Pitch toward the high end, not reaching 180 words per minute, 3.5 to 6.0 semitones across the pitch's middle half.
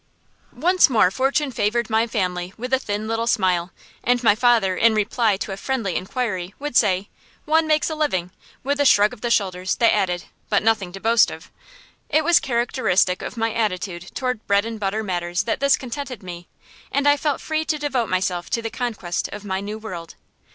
No: high, 220 Hz; average, 200 wpm; average, 5.0 semitones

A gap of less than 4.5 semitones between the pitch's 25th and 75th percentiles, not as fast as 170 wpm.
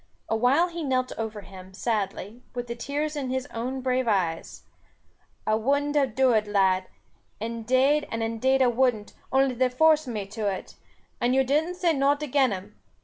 No: average, 4.0 semitones; average, 175 wpm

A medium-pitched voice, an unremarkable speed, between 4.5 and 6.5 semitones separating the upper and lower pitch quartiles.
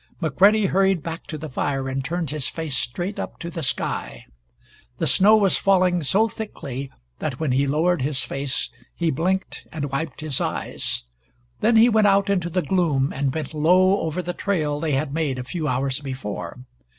Yes: medium, 160 Hz; average, 185 wpm; average, 5.1 semitones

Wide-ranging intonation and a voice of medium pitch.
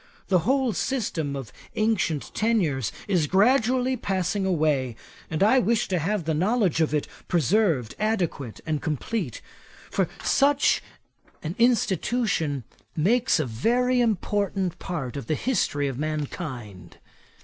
Yes: wide, 7.0 semitones; medium, 180 Hz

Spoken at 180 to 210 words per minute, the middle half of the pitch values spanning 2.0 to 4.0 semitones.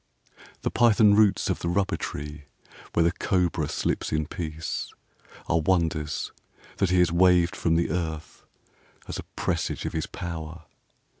No: average, 155 wpm; narrow, 2.5 semitones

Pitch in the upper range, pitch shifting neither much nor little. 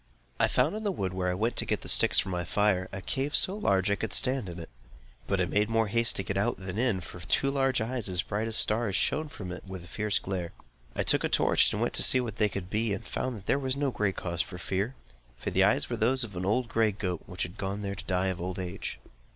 No: low, 100 Hz; average, 4.1 semitones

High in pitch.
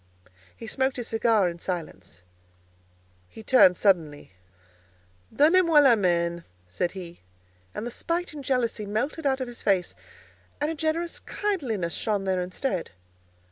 Yes: high, 220 Hz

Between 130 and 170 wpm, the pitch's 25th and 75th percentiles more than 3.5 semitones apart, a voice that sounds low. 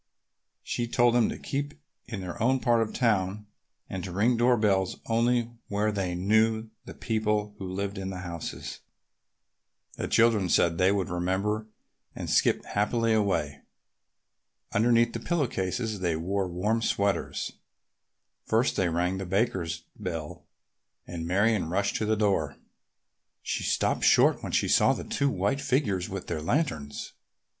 Yes: average, 150 wpm; average, 3.9 semitones; low, 105 Hz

